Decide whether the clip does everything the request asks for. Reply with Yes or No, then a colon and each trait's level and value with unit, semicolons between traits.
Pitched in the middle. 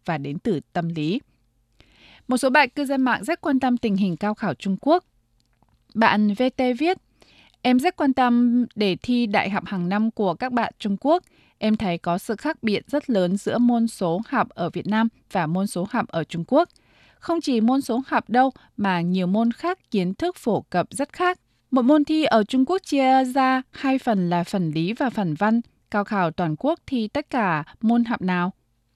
No: high, 225 Hz